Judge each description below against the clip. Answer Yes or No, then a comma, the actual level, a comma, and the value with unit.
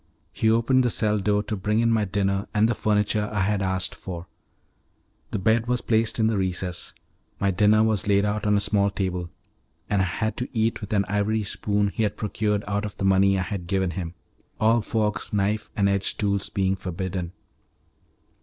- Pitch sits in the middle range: No, low, 105 Hz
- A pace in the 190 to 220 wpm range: Yes, average, 200 wpm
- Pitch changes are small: Yes, narrow, 2.0 semitones